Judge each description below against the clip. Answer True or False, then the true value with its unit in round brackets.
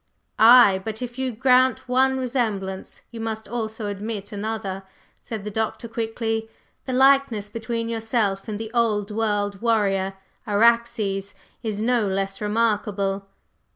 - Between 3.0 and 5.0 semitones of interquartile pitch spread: False (2.5 semitones)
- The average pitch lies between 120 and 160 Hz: False (220 Hz)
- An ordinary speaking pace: False (130 wpm)